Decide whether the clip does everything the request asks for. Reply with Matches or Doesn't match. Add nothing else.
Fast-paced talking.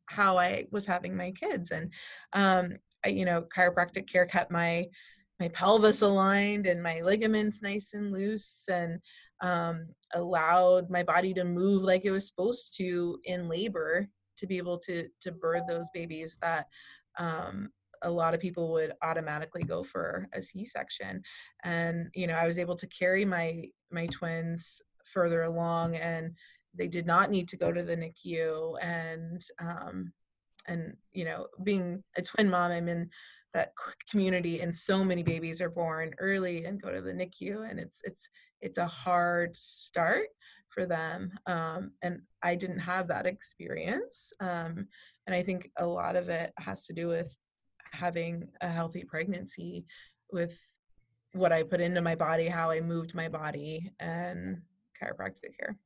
Doesn't match